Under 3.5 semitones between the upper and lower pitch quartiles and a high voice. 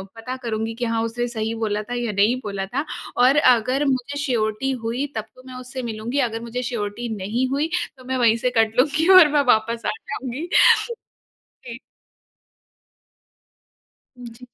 Yes: narrow, 2.6 semitones; high, 240 Hz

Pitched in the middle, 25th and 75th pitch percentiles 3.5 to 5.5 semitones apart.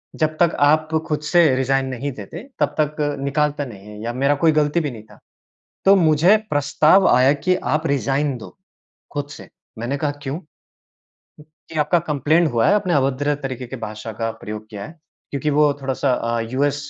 No: medium, 145 Hz; average, 3.1 semitones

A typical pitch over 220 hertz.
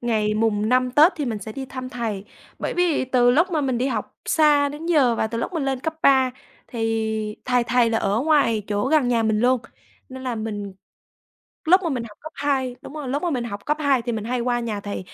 Yes: very high, 250 Hz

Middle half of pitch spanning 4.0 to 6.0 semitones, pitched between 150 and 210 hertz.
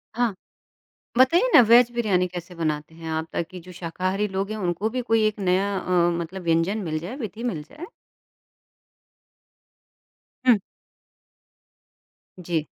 Yes: average, 4.4 semitones; medium, 185 Hz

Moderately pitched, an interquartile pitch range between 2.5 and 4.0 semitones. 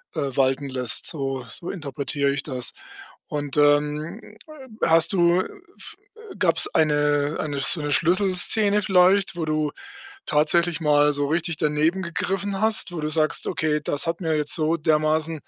Yes: medium, 155 Hz; average, 2.8 semitones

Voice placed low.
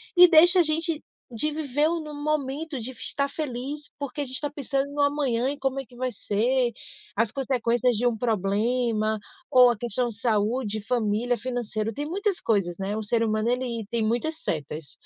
No: very high, 250 Hz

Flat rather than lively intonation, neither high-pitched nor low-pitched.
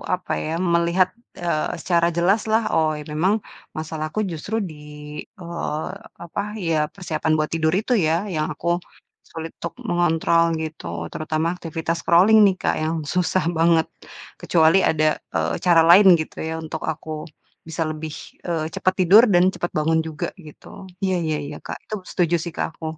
Yes: narrow, 2.1 semitones; medium, 165 Hz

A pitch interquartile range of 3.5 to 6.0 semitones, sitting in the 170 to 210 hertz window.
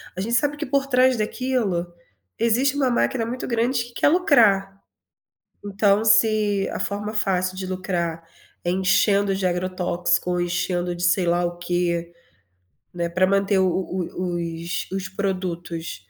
Yes: average, 4.0 semitones; high, 190 Hz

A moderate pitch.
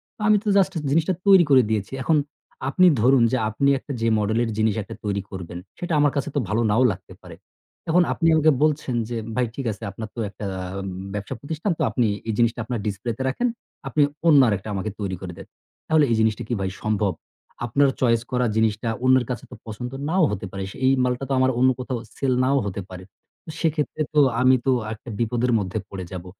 No: low, 120 Hz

